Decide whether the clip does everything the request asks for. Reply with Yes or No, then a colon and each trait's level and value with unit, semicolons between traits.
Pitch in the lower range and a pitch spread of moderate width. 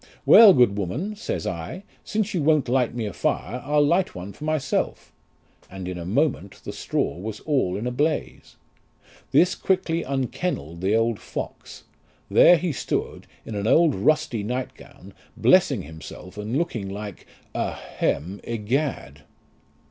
No: low, 120 Hz; wide, 7.8 semitones